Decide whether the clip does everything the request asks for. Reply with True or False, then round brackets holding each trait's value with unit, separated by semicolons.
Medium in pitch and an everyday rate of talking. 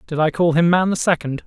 False (165 Hz; 285 wpm)